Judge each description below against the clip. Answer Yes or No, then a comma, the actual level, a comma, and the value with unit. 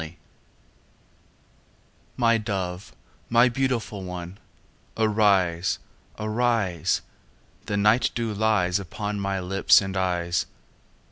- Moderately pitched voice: No, low, 100 Hz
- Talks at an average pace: No, slow, 90 wpm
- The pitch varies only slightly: No, average, 3.4 semitones